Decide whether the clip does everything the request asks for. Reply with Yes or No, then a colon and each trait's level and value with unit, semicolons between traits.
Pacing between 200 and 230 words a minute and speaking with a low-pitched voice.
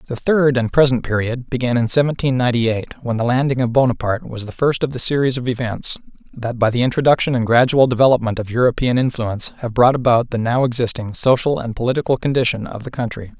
Yes: fast, 205 wpm; low, 125 Hz